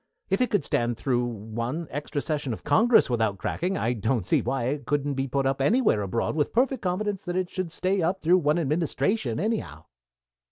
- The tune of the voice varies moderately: No, wide, 7.3 semitones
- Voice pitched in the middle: Yes, medium, 145 Hz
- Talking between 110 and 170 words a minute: No, average, 200 wpm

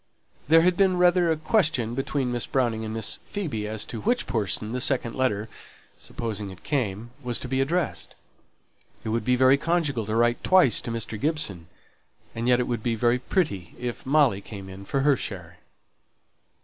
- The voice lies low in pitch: Yes, low, 120 Hz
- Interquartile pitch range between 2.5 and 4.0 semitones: No, average, 5.1 semitones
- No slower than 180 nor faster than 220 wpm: Yes, average, 190 wpm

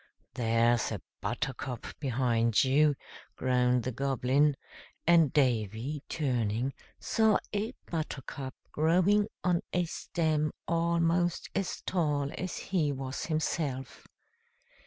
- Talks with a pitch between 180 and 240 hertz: No, medium, 145 Hz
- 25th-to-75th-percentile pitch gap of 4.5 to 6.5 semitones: Yes, average, 4.9 semitones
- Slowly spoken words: Yes, slow, 100 wpm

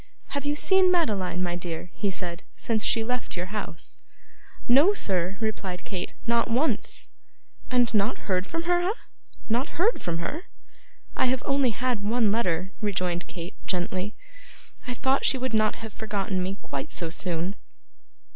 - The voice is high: Yes, high, 215 Hz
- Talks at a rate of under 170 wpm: Yes, average, 160 wpm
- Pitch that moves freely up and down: Yes, wide, 5.7 semitones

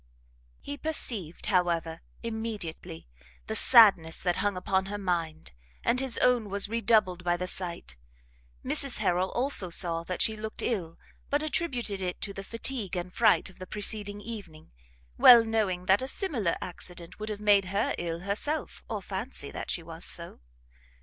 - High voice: Yes, high, 195 Hz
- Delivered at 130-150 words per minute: No, average, 165 wpm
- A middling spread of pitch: Yes, average, 4.2 semitones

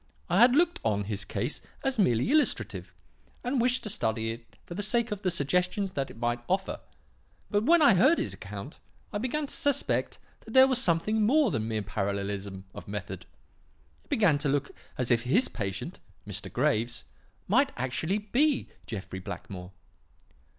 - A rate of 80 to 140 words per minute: No, average, 175 wpm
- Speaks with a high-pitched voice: No, medium, 175 Hz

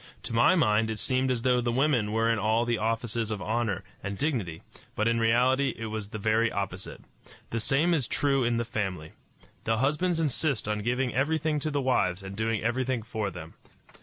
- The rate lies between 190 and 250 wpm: Yes, average, 200 wpm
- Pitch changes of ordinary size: Yes, average, 3.5 semitones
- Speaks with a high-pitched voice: No, low, 115 Hz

